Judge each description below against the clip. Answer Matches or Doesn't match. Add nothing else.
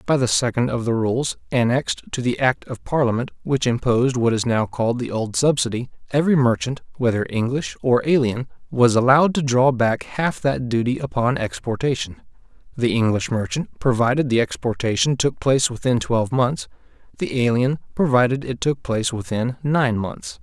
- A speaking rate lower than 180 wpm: Matches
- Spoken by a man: Matches